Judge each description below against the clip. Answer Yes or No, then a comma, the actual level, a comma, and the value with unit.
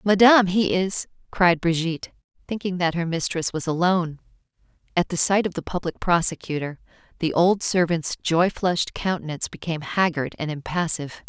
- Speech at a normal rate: Yes, average, 150 wpm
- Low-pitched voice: No, medium, 175 Hz